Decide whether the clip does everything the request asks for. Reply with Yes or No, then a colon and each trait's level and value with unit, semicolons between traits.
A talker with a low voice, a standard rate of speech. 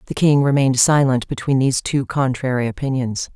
Yes: low, 130 Hz; average, 160 wpm